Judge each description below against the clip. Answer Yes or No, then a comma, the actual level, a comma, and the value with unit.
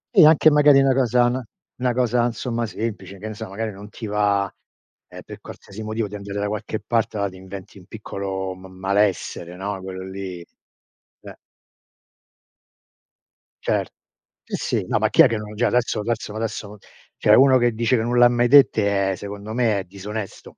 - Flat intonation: No, average, 3.3 semitones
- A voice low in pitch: Yes, low, 105 Hz